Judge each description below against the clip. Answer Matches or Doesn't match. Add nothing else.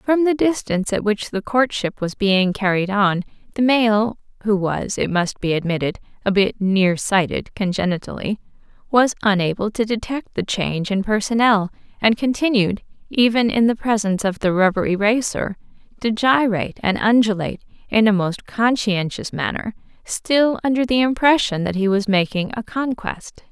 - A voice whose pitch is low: Doesn't match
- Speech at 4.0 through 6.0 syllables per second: Matches